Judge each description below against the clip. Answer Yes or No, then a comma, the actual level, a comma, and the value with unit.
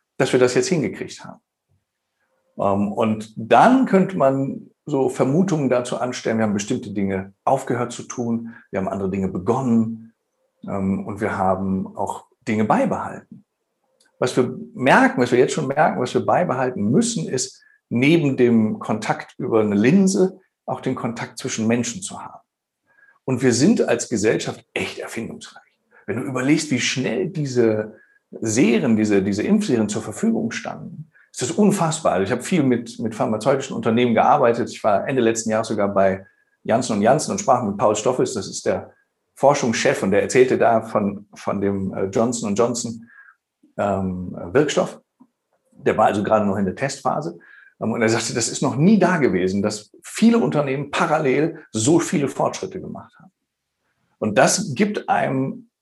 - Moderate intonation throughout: No, wide, 6.5 semitones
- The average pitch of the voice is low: Yes, low, 125 Hz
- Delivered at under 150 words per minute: No, average, 160 wpm